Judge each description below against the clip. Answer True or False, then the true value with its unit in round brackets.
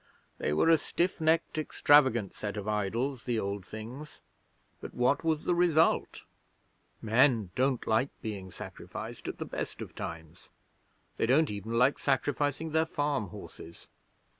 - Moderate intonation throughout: False (5.9 semitones)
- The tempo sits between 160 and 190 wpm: False (145 wpm)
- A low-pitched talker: True (125 Hz)